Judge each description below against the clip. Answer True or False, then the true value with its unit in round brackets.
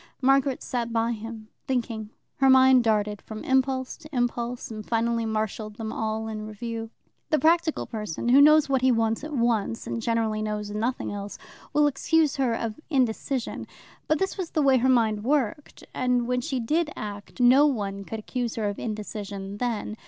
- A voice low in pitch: False (235 Hz)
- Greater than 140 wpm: True (180 wpm)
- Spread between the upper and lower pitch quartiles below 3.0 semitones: False (3.4 semitones)